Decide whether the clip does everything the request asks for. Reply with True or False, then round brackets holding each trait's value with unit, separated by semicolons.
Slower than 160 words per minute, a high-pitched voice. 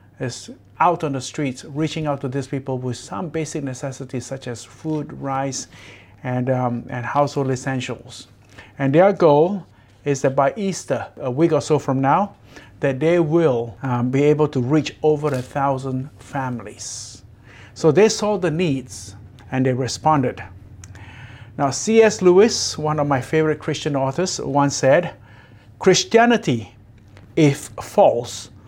False (145 wpm; 135 Hz)